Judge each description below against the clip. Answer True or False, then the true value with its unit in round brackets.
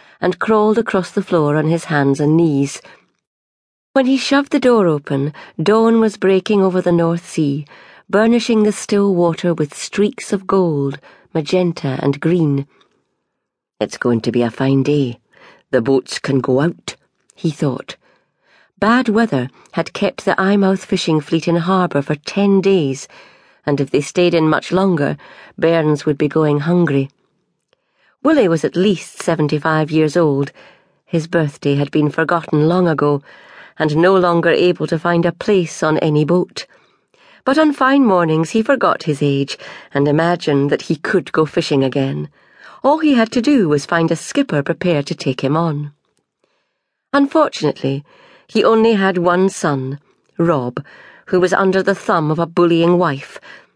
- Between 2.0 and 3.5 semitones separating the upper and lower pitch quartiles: False (4.9 semitones)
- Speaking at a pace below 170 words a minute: True (160 wpm)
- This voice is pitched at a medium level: True (170 Hz)